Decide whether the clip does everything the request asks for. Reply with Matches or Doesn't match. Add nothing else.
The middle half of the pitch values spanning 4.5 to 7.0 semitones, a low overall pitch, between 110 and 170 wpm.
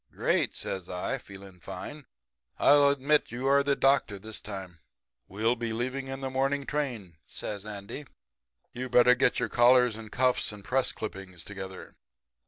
Matches